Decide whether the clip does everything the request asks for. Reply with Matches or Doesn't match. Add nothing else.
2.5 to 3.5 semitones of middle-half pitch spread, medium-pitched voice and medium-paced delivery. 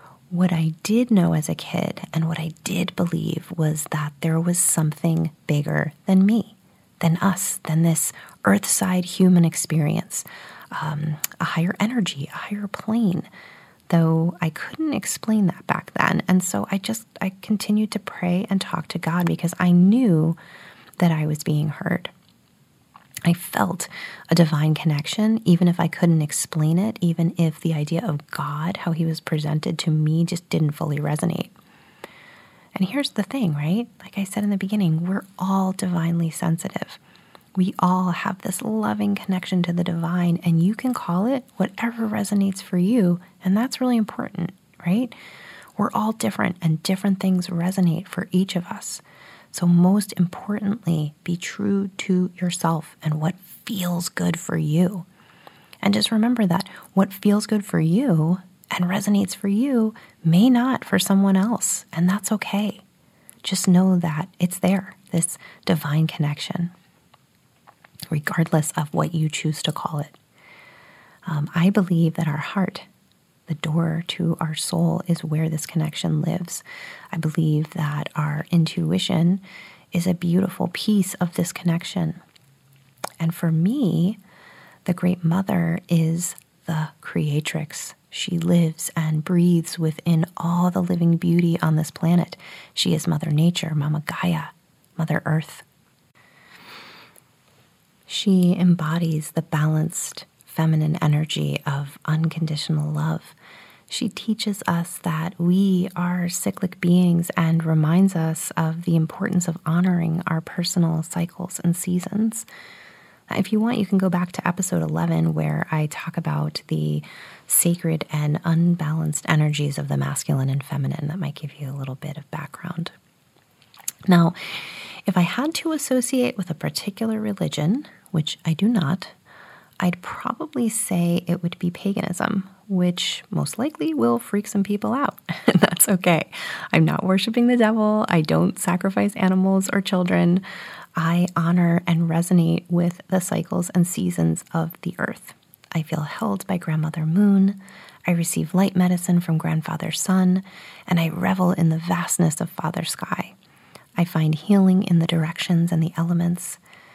Matches